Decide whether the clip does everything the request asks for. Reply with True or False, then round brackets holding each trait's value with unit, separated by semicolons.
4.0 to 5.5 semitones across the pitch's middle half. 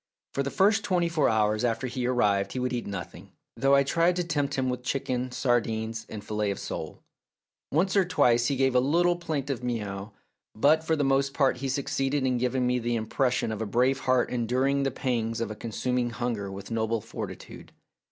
False (3.4 semitones)